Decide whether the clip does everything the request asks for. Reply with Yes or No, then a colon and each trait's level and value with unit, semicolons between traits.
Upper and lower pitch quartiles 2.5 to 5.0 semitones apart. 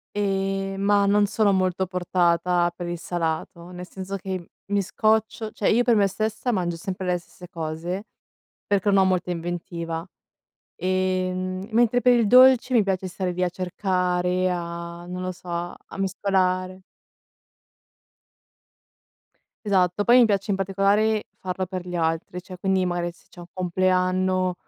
No: narrow, 1.9 semitones